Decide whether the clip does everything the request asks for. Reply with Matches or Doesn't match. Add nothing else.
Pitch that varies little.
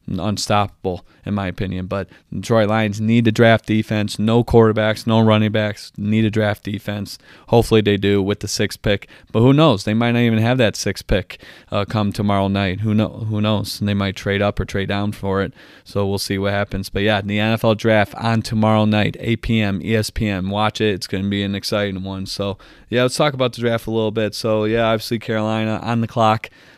Matches